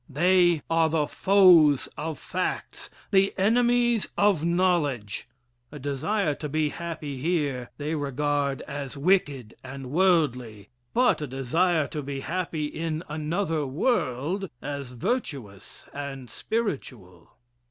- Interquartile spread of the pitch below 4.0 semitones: No, average, 4.7 semitones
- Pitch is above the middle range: No, medium, 150 Hz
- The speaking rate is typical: No, slow, 120 wpm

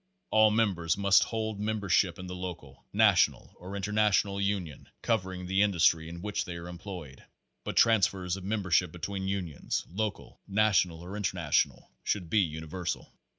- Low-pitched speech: Yes, very low, 95 Hz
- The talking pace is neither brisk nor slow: Yes, average, 150 wpm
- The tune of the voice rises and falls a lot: No, average, 3.0 semitones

